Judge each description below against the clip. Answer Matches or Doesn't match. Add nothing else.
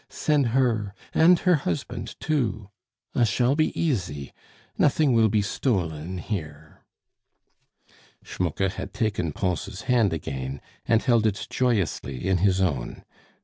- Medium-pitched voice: Doesn't match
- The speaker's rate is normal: Doesn't match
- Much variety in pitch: Matches